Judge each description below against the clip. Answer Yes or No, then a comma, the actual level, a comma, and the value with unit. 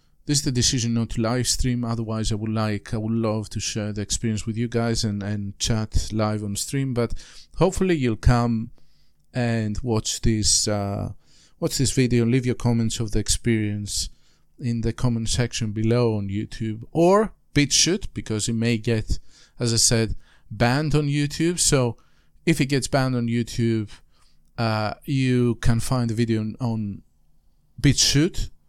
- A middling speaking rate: Yes, average, 170 wpm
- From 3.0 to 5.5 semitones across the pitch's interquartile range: No, narrow, 2.6 semitones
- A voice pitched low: Yes, low, 115 Hz